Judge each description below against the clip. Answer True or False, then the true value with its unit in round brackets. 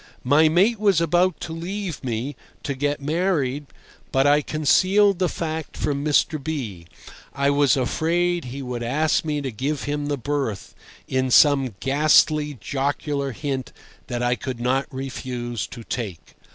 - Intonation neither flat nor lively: True (3.4 semitones)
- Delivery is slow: False (150 wpm)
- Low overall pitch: False (145 Hz)